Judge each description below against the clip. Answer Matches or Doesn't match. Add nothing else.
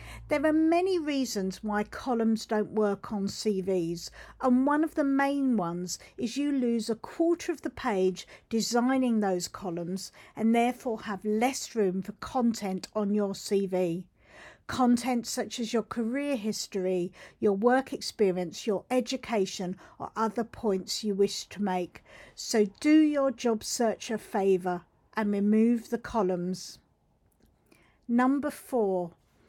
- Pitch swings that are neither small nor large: Matches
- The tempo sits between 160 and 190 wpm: Doesn't match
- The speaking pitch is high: Matches